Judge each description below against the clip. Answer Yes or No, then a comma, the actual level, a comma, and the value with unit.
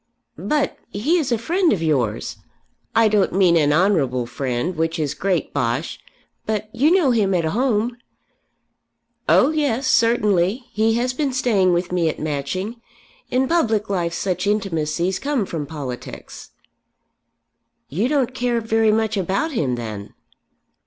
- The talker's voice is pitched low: No, high, 205 Hz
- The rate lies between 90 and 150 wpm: Yes, average, 145 wpm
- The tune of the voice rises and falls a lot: Yes, wide, 6.7 semitones